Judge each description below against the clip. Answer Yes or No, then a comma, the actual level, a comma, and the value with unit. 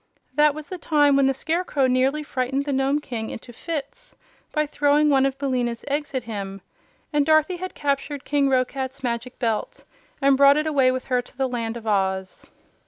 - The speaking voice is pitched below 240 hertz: No, very high, 275 Hz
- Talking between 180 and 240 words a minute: Yes, average, 190 wpm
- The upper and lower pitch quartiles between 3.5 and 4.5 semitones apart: No, average, 2.8 semitones